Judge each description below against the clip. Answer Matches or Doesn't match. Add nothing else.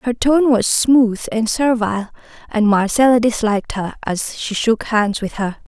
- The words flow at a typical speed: Matches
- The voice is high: Matches